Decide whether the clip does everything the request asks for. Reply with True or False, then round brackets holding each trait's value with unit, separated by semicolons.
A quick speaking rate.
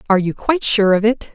True (265 wpm)